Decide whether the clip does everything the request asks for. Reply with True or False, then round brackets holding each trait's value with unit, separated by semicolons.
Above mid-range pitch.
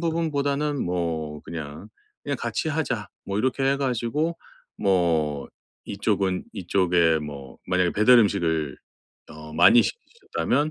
False (95 Hz)